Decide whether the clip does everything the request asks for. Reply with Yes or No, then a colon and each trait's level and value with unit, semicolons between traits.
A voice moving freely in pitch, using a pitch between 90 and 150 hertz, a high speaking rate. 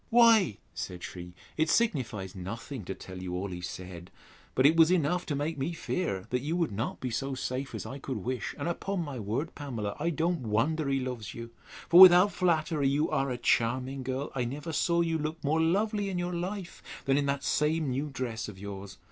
Yes: wide, 6.3 semitones; medium, 140 Hz; fast, 215 wpm